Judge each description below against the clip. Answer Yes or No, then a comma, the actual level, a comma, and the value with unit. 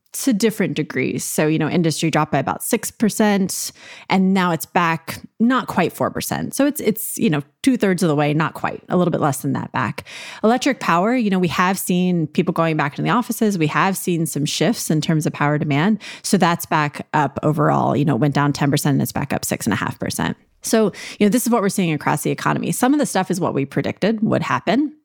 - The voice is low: No, medium, 180 Hz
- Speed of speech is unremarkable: No, fast, 245 wpm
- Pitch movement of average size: No, wide, 6.3 semitones